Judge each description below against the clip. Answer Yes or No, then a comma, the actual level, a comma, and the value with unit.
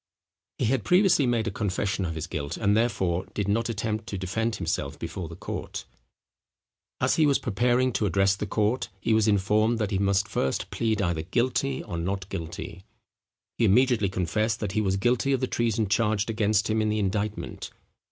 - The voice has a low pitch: Yes, low, 105 Hz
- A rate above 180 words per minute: Yes, average, 190 wpm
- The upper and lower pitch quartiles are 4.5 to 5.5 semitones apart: No, average, 3.1 semitones